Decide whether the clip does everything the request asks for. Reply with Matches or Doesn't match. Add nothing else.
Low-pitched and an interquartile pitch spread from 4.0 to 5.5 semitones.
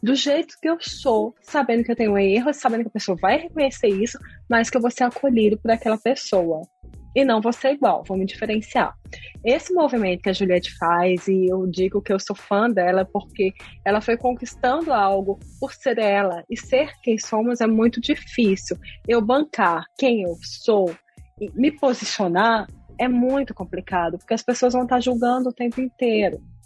Doesn't match